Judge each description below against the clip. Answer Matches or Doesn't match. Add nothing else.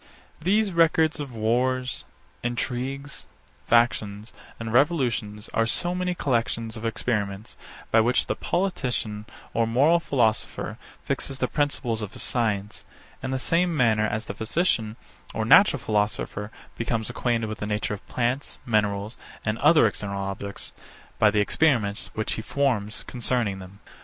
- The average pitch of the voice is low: Matches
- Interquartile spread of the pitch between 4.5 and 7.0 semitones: Doesn't match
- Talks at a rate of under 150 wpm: Matches